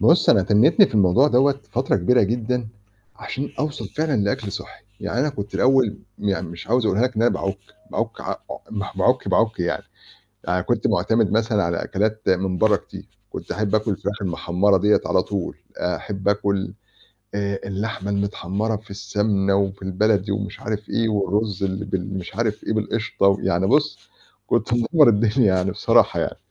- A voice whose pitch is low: Yes, low, 105 Hz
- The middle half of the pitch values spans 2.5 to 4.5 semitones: Yes, average, 2.8 semitones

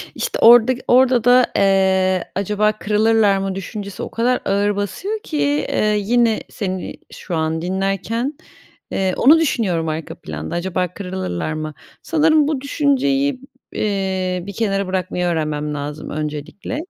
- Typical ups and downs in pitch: Yes, average, 4.9 semitones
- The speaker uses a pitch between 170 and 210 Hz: Yes, high, 195 Hz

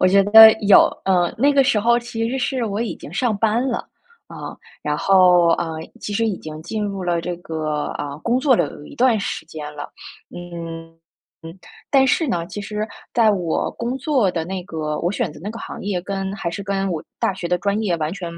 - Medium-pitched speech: No, high, 195 Hz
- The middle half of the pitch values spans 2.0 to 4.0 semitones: No, average, 4.8 semitones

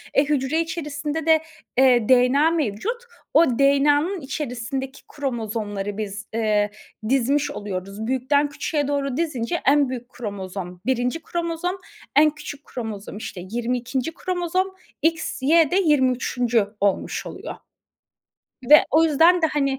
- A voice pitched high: Yes, very high, 270 Hz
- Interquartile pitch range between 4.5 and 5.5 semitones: Yes, average, 4.9 semitones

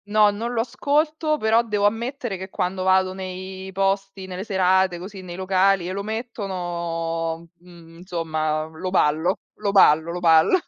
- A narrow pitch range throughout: No, average, 3.0 semitones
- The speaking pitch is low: No, high, 190 Hz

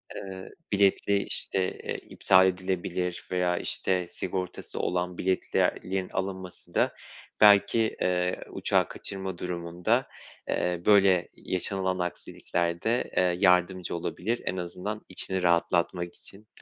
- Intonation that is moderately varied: No, narrow, 1.4 semitones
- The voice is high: No, very low, 90 Hz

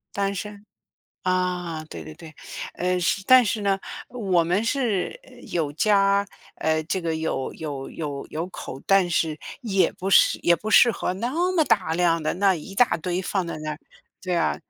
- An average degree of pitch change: Yes, average, 3.7 semitones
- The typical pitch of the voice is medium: Yes, medium, 180 Hz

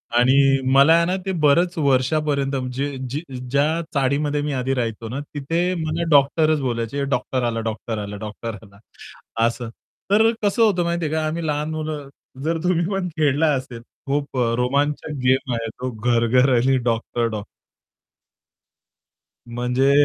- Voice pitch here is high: No, medium, 140 Hz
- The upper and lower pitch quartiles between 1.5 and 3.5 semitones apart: No, average, 4.1 semitones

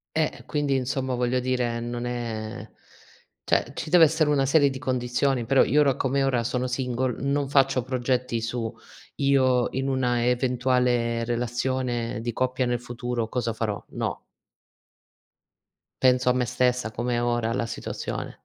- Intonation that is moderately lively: No, narrow, 1.7 semitones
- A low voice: Yes, low, 125 Hz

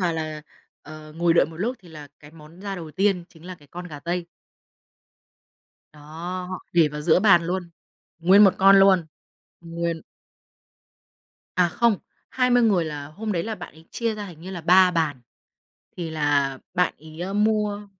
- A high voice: No, medium, 175 Hz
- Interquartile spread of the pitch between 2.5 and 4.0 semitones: Yes, average, 3.7 semitones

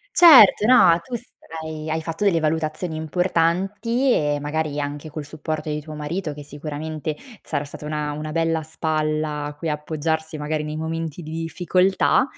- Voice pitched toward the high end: No, medium, 155 Hz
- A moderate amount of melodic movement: No, narrow, 1.6 semitones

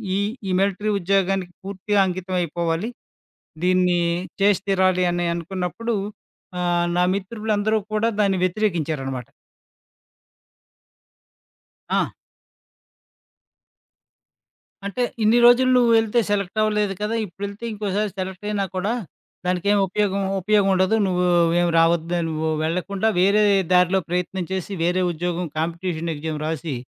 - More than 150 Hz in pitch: Yes, medium, 185 Hz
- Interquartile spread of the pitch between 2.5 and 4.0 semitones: Yes, average, 2.9 semitones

